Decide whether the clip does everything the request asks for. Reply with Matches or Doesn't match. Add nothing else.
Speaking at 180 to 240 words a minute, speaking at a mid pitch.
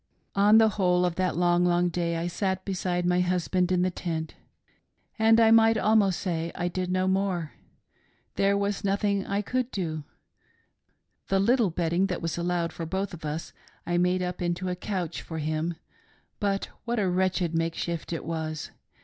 Matches